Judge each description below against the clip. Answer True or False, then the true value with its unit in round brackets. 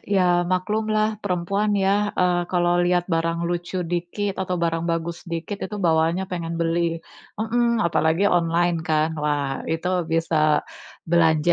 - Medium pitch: True (175 Hz)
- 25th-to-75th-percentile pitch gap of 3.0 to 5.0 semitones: False (2.5 semitones)